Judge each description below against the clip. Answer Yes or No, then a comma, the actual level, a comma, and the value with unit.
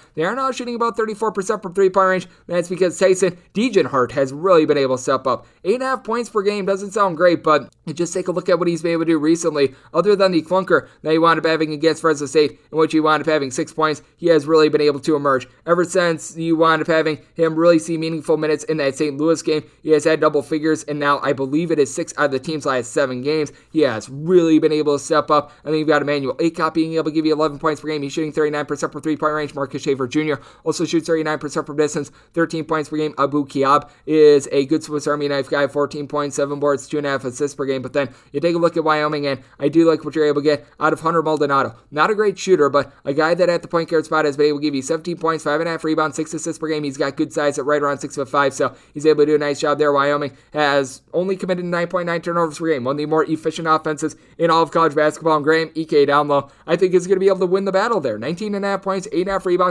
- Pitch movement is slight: Yes, narrow, 2.1 semitones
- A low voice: No, medium, 155 Hz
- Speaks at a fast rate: Yes, fast, 280 wpm